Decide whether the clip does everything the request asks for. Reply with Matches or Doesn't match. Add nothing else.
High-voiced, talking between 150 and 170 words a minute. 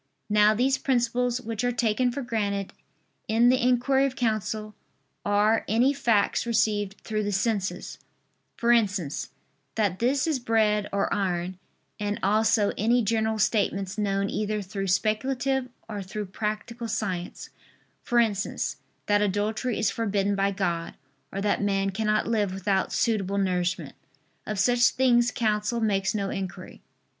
Doesn't match